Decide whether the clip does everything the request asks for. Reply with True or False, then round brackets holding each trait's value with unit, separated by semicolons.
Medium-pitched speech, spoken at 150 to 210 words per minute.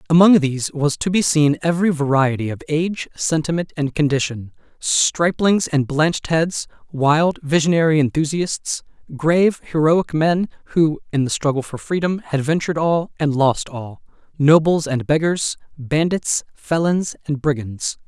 False (155 Hz; 135 wpm)